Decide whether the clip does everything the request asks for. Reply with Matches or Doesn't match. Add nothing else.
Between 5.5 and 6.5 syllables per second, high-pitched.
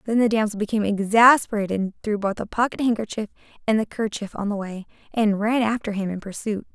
Matches